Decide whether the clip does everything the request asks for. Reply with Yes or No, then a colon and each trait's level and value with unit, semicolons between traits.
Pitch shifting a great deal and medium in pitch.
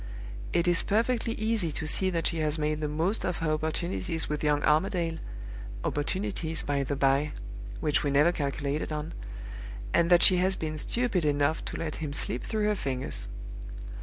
No: average, 3.4 semitones; medium, 160 Hz